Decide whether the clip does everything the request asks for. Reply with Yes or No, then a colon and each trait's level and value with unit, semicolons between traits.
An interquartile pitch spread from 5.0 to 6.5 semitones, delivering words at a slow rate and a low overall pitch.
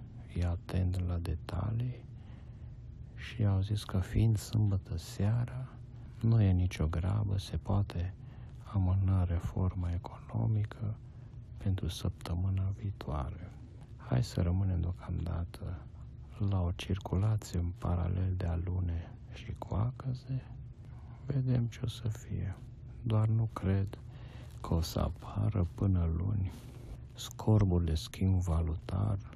No: average, 4.4 semitones; slow, 110 wpm; low, 105 Hz